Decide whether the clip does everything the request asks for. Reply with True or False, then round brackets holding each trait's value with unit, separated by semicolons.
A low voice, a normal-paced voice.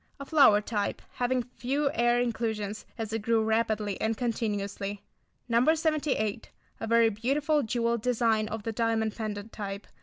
False (225 Hz; 150 wpm)